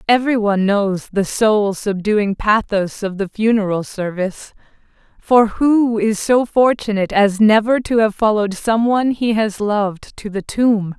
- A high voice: Yes, high, 210 Hz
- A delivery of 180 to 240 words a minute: No, average, 160 wpm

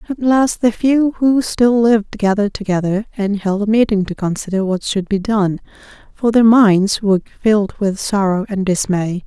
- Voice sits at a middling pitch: No, high, 210 Hz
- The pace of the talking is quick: No, average, 180 wpm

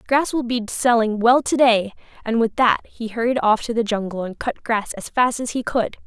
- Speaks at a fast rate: Yes, fast, 235 wpm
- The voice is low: No, high, 230 Hz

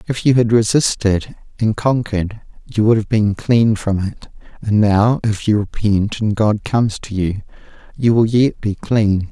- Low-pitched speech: Yes, low, 110 Hz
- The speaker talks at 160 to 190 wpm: Yes, average, 180 wpm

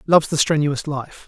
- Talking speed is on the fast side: No, average, 190 wpm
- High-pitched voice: No, medium, 150 Hz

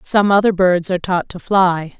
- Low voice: No, medium, 185 Hz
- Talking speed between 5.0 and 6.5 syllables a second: No, 4.8 syllables/s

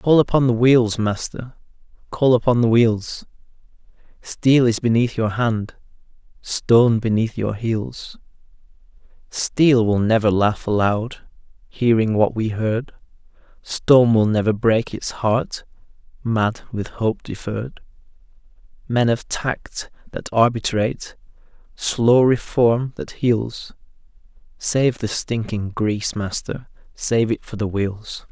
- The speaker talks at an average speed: No, slow, 120 wpm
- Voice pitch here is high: No, low, 115 Hz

